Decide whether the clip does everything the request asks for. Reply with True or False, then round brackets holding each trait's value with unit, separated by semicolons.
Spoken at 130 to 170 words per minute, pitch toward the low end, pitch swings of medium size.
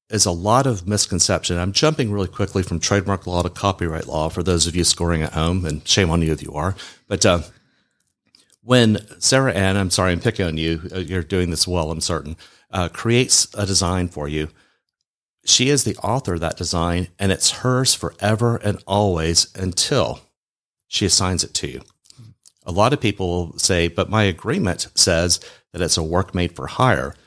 False (195 wpm; 90 Hz; 3.4 semitones)